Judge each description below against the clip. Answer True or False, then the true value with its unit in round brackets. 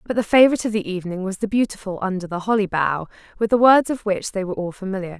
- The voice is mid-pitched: False (200 Hz)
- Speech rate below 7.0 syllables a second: False (7.2 syllables/s)